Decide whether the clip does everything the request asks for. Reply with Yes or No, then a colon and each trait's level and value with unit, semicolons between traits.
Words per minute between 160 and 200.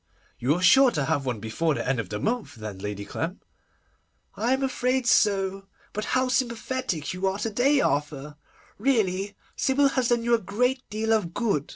Yes: average, 190 wpm